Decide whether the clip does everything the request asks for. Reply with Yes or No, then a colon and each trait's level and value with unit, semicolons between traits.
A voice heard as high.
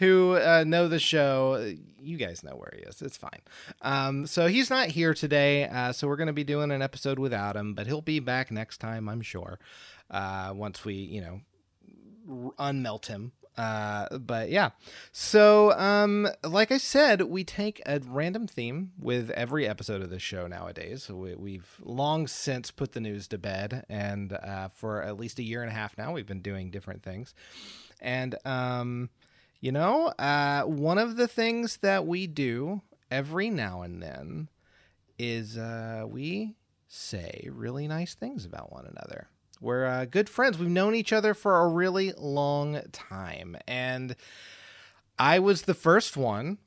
No: low, 135 Hz